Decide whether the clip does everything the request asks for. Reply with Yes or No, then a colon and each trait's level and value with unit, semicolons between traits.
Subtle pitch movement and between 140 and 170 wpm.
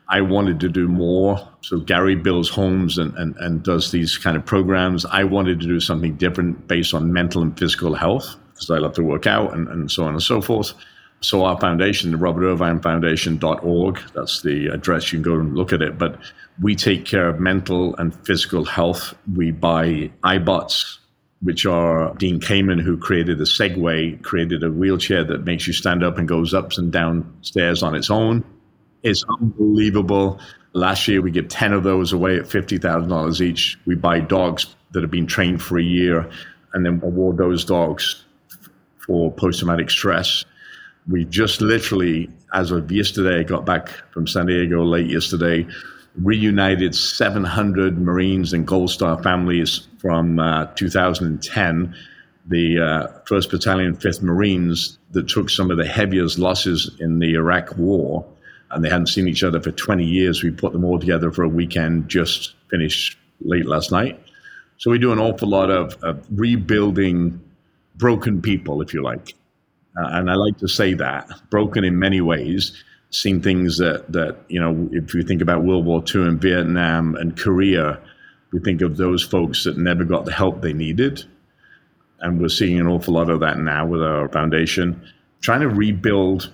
No: narrow, 2.3 semitones; average, 180 wpm